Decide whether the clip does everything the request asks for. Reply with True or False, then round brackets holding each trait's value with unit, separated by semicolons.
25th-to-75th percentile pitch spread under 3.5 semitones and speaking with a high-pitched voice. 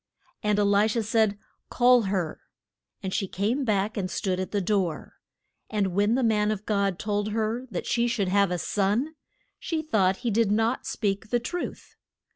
True (2.7 semitones; 210 Hz)